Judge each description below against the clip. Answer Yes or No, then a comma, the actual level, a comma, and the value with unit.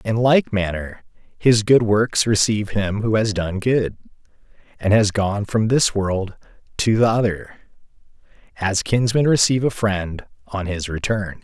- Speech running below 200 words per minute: Yes, average, 145 wpm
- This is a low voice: Yes, low, 105 Hz